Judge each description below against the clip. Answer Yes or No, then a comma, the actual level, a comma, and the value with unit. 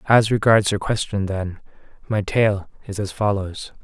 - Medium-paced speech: Yes, average, 155 wpm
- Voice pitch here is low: Yes, low, 100 Hz